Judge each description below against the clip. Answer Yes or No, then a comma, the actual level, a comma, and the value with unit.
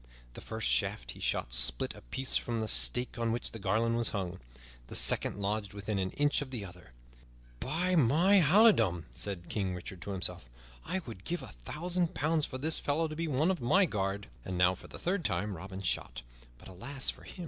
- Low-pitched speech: Yes, low, 110 Hz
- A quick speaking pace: Yes, fast, 210 wpm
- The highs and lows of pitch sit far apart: Yes, wide, 8.2 semitones